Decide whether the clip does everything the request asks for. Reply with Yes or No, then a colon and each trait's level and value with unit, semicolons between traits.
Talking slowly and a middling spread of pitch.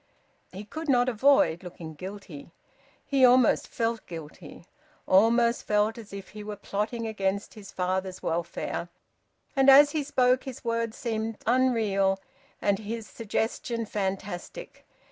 Yes: slow, 130 wpm; average, 3.9 semitones